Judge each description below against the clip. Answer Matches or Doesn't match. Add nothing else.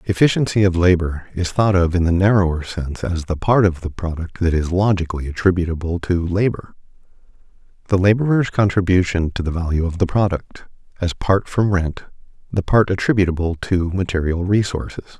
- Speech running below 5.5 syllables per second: Doesn't match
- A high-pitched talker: Doesn't match